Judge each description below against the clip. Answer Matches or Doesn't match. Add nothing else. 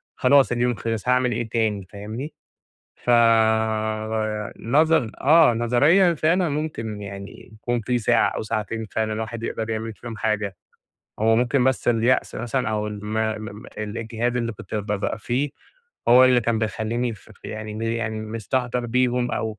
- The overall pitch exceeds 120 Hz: Doesn't match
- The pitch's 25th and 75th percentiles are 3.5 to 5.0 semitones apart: Doesn't match